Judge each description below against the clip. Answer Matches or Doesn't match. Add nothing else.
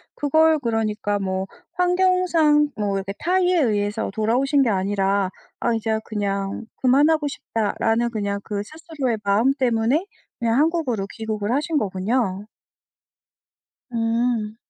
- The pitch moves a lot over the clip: Matches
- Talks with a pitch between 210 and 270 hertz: Matches